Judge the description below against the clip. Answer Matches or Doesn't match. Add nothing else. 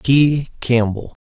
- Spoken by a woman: Doesn't match